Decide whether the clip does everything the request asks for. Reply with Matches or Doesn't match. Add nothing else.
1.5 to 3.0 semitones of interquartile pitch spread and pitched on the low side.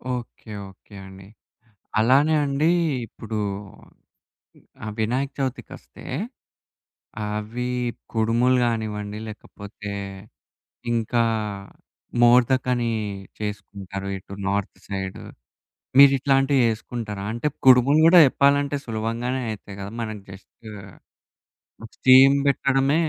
Doesn't match